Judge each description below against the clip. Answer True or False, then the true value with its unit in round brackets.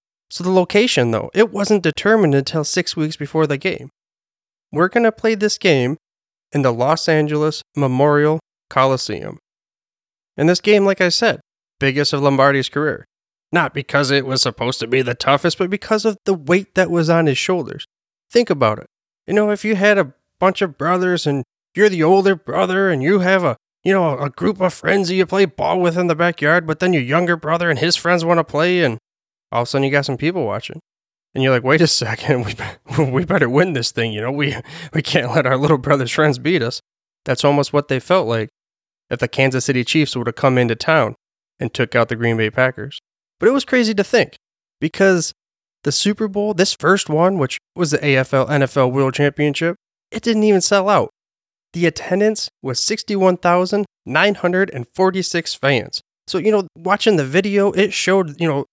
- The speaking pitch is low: False (165 Hz)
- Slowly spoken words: False (200 wpm)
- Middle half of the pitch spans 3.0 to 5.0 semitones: False (5.6 semitones)